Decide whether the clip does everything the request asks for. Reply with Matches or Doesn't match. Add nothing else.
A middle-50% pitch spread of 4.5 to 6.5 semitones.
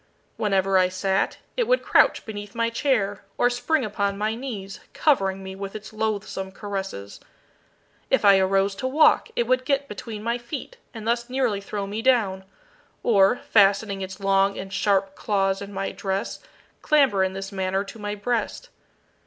Doesn't match